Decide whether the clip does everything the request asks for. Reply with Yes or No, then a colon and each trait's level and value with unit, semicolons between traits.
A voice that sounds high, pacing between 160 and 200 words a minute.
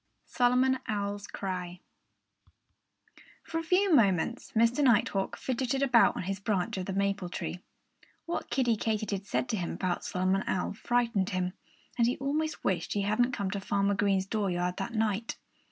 Yes: high, 205 Hz; average, 165 wpm